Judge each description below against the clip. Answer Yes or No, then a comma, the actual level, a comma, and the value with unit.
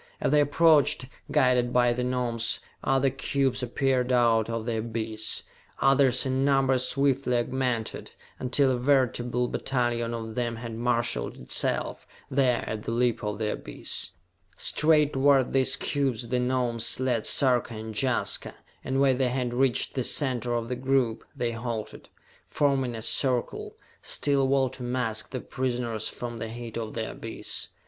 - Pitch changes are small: Yes, narrow, 2.3 semitones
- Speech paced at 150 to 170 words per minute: Yes, average, 155 wpm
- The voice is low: Yes, low, 125 Hz